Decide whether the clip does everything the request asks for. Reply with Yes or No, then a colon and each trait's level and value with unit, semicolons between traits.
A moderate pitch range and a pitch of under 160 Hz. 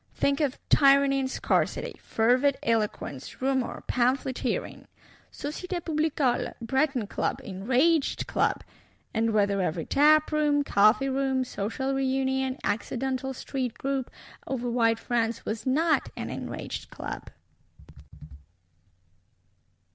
No: average, 3.2 semitones; very high, 265 Hz